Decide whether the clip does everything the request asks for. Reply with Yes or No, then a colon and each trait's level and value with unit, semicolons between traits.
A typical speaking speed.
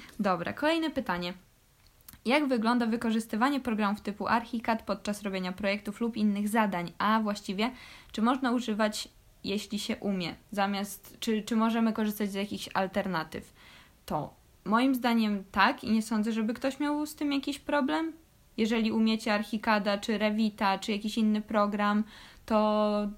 Yes: average, 140 wpm